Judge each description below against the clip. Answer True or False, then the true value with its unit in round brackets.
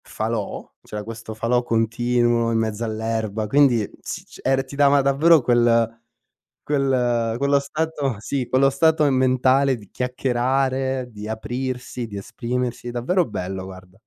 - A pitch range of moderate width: True (3.0 semitones)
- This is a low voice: True (120 Hz)